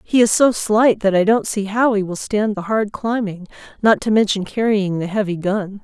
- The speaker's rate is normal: No, fast, 225 wpm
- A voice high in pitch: Yes, high, 205 Hz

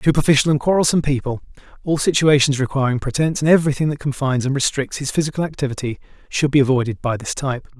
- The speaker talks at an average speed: Yes, average, 175 wpm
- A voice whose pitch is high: No, medium, 140 Hz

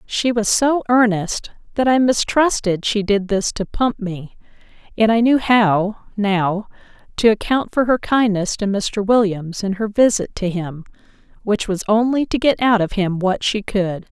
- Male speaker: No, female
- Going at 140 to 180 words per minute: Yes, average, 175 wpm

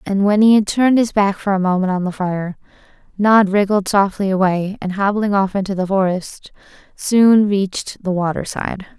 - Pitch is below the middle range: No, high, 195 Hz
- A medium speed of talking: Yes, average, 185 wpm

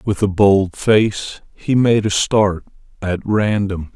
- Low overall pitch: Yes, low, 100 Hz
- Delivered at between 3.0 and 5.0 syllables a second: Yes, 3.3 syllables/s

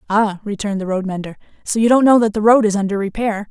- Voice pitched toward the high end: Yes, high, 210 Hz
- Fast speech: Yes, fast, 255 wpm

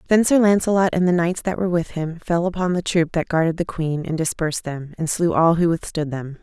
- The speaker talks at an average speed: No, fast, 250 wpm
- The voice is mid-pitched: Yes, medium, 170 Hz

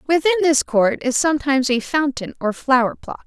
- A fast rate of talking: No, average, 185 wpm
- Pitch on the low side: No, very high, 280 Hz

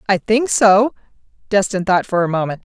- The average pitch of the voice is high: Yes, high, 200 Hz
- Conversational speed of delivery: Yes, average, 180 wpm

